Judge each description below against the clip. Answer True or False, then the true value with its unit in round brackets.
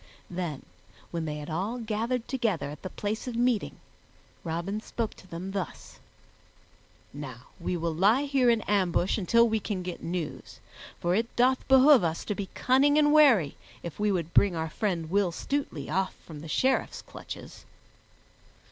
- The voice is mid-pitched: False (195 Hz)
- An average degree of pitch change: False (5.8 semitones)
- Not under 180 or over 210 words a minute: False (165 wpm)